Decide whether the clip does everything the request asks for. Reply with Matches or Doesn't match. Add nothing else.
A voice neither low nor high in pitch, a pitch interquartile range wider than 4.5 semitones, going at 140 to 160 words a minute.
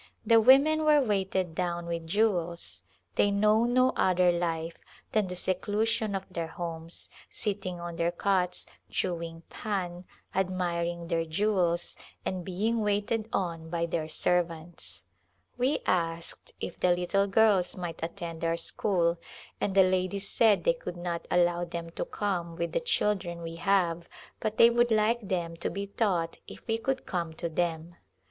Doesn't match